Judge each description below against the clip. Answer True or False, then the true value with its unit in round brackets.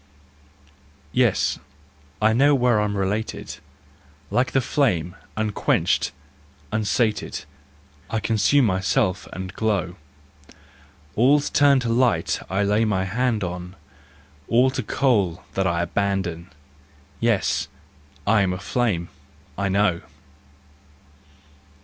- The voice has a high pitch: False (105 Hz)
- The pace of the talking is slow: True (105 wpm)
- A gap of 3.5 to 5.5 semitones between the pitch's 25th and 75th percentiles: True (4.4 semitones)